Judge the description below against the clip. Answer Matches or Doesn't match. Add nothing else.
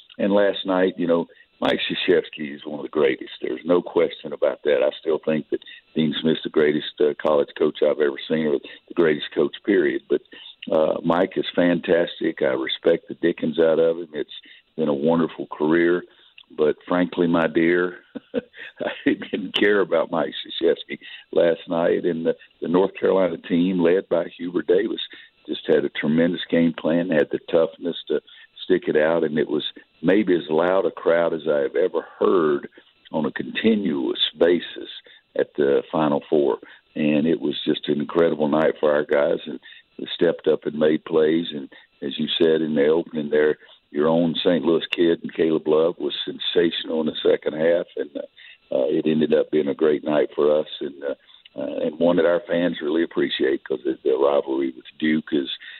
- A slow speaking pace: Doesn't match